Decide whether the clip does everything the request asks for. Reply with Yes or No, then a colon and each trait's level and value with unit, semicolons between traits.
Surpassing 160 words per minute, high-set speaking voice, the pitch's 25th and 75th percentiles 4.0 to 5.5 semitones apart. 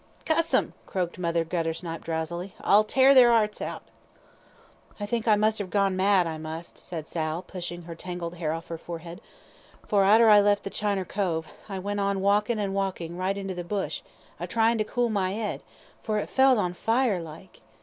No: average, 195 wpm; high, 195 Hz; average, 3.5 semitones